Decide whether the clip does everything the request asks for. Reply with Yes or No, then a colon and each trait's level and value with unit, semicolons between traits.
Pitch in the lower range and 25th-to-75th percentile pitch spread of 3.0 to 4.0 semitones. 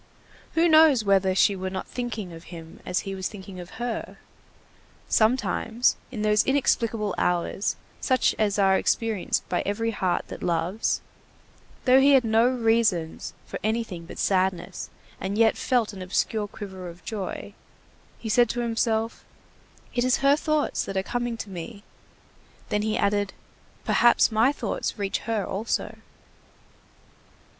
No: high, 215 Hz; average, 3.7 semitones